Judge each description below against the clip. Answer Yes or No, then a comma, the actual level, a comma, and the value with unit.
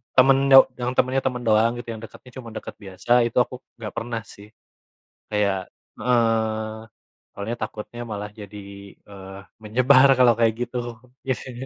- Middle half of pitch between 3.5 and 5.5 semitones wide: No, average, 2.8 semitones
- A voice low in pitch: Yes, low, 115 Hz